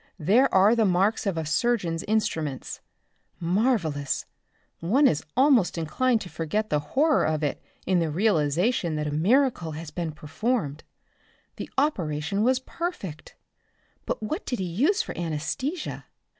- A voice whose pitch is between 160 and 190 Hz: Yes, medium, 185 Hz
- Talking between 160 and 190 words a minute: No, average, 145 wpm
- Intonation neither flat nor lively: No, wide, 7.6 semitones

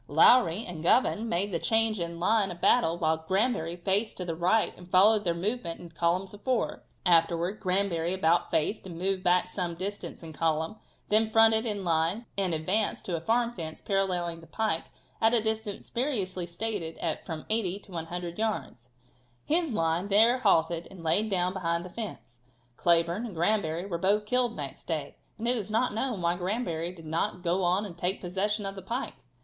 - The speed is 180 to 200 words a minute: Yes, average, 190 wpm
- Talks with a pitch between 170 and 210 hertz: Yes, medium, 185 Hz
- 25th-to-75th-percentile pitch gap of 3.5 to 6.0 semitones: Yes, average, 4.3 semitones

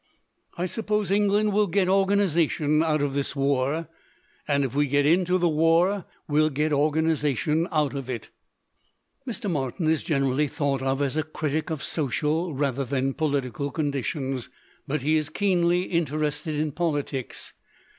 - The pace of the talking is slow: No, average, 150 wpm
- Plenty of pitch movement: No, average, 3.3 semitones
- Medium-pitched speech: Yes, medium, 155 Hz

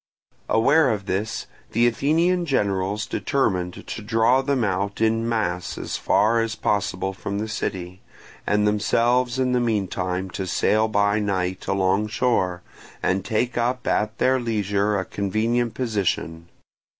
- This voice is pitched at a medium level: No, low, 105 Hz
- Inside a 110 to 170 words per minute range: Yes, average, 140 wpm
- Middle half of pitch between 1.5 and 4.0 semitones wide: Yes, average, 3.6 semitones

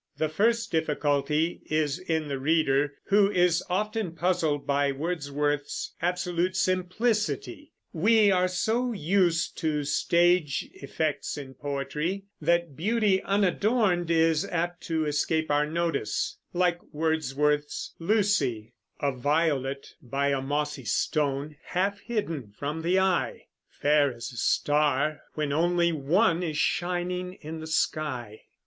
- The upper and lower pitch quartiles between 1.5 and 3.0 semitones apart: No, average, 3.8 semitones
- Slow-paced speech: Yes, slow, 125 wpm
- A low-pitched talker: No, medium, 160 Hz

